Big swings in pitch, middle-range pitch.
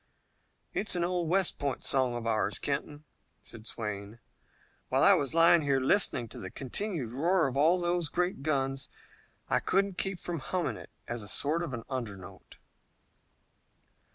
Yes: wide, 6.5 semitones; medium, 145 Hz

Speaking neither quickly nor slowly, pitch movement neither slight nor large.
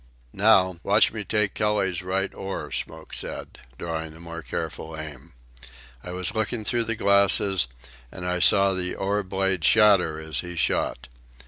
Yes: average, 155 wpm; average, 3.2 semitones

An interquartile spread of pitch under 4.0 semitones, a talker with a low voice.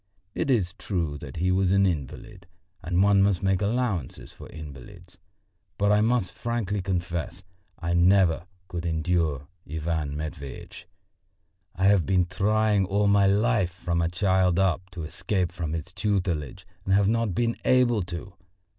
Yes: average, 3.0 semitones; very low, 90 Hz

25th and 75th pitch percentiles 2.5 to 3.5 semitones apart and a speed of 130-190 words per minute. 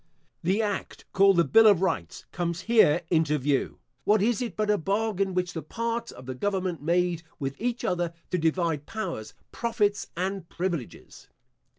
No: average, 4.2 semitones; average, 170 wpm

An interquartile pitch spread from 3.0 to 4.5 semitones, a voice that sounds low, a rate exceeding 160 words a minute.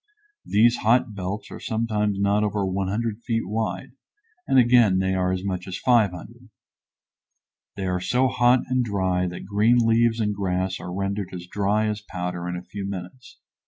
Yes: average, 3.6 semitones; low, 100 Hz; average, 170 wpm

